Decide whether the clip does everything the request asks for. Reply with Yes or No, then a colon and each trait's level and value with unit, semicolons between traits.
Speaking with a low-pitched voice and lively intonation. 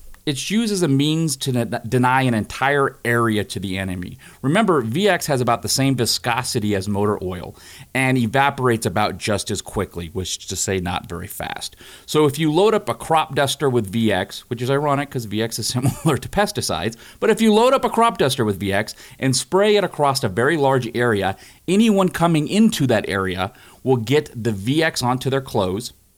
Yes: low, 125 Hz; wide, 5.9 semitones